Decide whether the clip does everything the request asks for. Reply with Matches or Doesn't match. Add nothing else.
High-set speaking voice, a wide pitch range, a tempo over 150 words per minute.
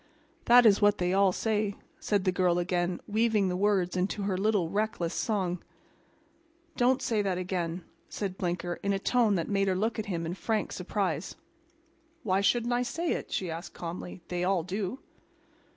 Doesn't match